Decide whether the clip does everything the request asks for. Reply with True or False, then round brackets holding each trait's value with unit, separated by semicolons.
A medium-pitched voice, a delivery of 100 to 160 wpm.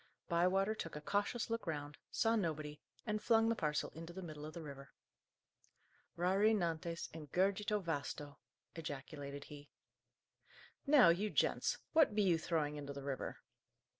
True (165 Hz; 150 wpm)